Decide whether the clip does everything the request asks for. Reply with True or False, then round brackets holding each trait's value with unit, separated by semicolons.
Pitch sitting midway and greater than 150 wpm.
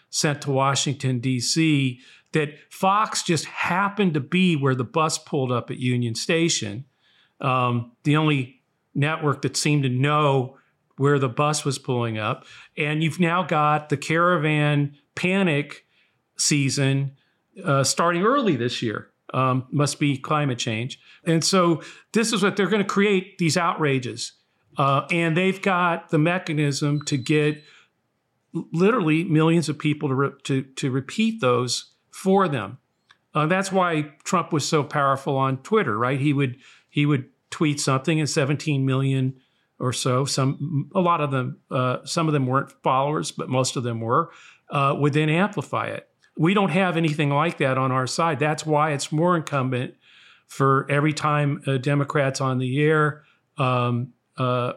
True (145 Hz; 160 wpm)